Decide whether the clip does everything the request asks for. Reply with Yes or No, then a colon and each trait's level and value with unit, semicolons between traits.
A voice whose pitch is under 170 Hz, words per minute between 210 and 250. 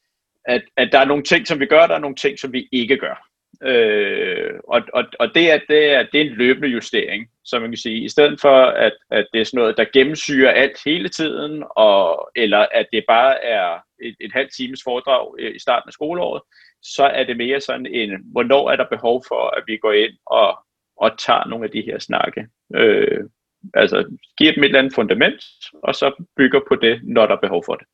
Yes: medium, 140 Hz; fast, 225 wpm